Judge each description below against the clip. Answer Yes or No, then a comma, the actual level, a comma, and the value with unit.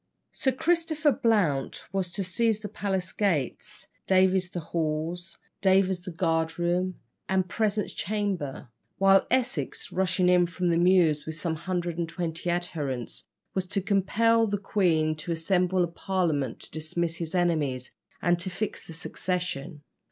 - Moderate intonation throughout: Yes, average, 3.0 semitones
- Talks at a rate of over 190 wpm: No, average, 150 wpm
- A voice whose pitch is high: No, medium, 180 Hz